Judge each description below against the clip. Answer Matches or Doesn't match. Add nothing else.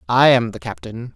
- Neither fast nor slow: Doesn't match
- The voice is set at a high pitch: Doesn't match